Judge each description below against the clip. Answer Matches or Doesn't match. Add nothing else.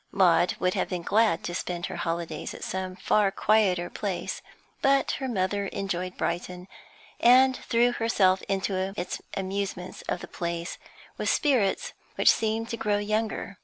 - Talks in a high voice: Matches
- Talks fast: Doesn't match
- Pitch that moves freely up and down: Doesn't match